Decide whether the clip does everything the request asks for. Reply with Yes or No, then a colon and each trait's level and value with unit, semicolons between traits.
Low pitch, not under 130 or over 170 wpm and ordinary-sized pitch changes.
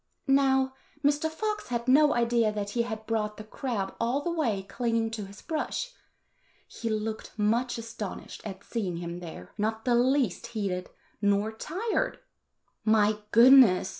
No: high, 225 Hz; average, 150 wpm; average, 3.6 semitones